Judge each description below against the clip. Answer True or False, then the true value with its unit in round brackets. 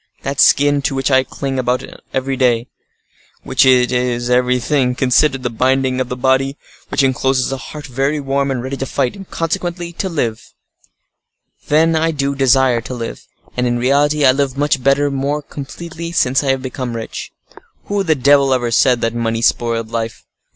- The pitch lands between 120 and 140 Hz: True (135 Hz)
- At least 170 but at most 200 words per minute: True (180 wpm)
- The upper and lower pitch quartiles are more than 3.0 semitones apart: False (2.4 semitones)